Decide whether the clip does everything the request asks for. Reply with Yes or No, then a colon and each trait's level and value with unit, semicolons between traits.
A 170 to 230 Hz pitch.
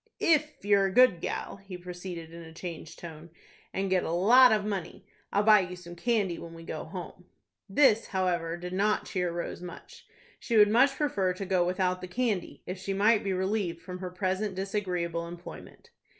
Yes: medium, 185 Hz